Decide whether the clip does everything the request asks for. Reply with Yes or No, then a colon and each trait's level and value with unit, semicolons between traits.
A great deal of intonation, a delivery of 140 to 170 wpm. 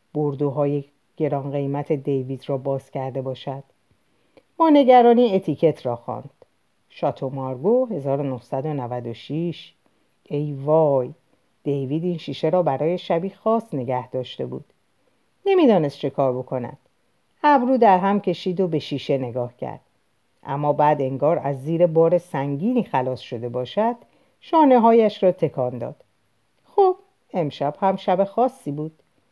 No: wide, 5.8 semitones; average, 125 wpm